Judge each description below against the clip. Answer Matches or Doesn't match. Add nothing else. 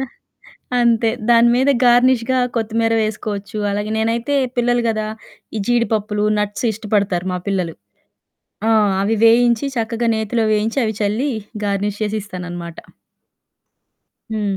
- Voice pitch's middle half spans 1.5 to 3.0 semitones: Matches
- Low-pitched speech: Doesn't match